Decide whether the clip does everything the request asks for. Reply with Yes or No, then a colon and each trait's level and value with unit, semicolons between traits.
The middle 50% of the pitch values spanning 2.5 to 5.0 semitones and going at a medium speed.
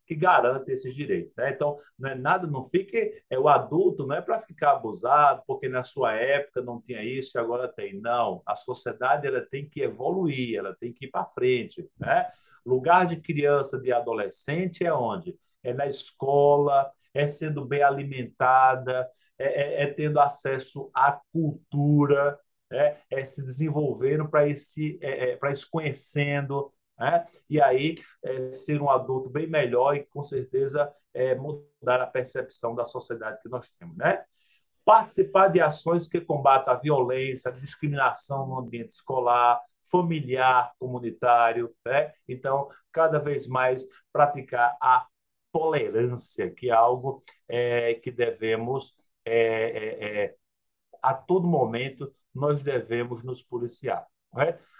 Yes: average, 3.3 semitones; average, 145 wpm